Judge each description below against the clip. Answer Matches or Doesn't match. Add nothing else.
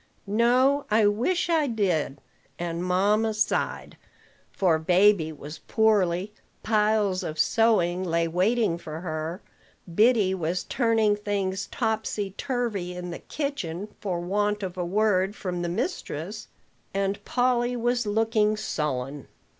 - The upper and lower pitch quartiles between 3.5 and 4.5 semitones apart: Matches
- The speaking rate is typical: Doesn't match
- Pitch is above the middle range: Matches